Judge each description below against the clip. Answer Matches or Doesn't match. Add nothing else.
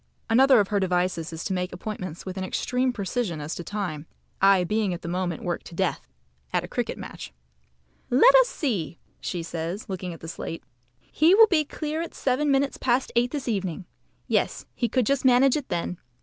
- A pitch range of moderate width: Doesn't match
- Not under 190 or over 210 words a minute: Matches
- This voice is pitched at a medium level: Doesn't match